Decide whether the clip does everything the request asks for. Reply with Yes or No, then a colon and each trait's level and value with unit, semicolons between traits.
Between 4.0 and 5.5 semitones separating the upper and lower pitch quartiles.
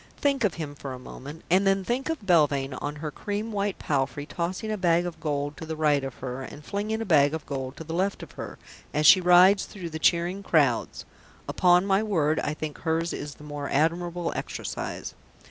Yes: average, 4.7 semitones